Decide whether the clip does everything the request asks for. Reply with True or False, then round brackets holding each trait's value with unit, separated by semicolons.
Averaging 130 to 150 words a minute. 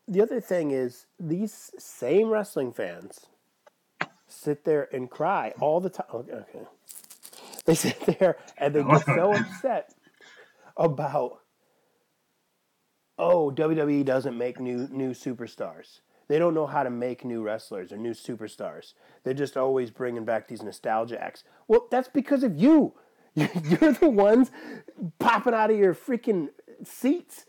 True (145 wpm)